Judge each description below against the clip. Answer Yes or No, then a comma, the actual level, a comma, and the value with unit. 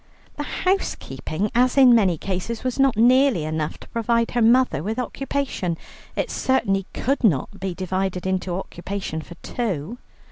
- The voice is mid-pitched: No, high, 210 Hz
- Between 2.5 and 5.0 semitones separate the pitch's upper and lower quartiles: No, wide, 5.5 semitones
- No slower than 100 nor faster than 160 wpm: Yes, average, 150 wpm